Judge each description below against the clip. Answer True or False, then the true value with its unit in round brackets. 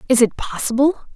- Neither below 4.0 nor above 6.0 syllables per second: True (5.9 syllables/s)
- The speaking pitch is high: True (245 Hz)